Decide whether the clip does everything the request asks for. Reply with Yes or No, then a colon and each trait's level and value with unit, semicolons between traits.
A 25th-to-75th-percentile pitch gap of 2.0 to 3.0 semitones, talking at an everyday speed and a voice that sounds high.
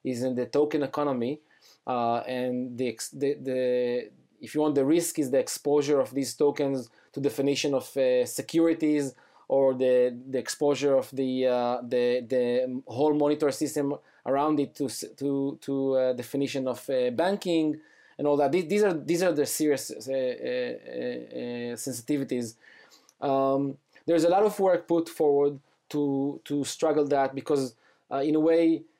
No: average, 2.7 semitones; average, 165 wpm; medium, 140 Hz